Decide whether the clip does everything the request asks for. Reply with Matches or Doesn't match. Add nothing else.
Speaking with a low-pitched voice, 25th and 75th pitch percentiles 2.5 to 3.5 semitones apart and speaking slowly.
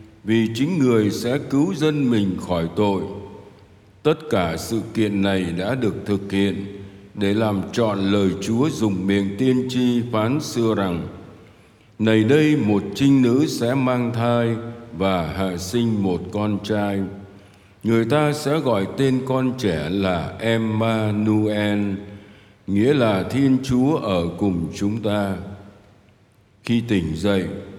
Matches